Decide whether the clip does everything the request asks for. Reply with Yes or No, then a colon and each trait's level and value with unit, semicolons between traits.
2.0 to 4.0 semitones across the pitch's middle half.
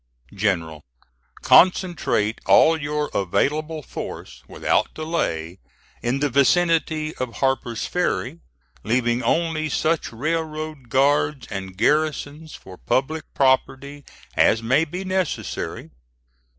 No: average, 5.1 semitones